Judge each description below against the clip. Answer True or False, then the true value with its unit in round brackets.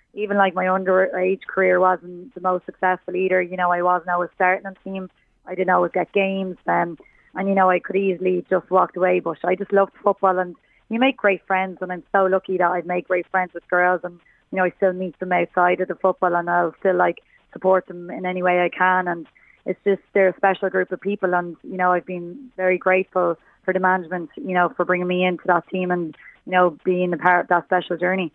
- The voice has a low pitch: False (185 Hz)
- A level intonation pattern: True (0.9 semitones)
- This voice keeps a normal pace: False (240 wpm)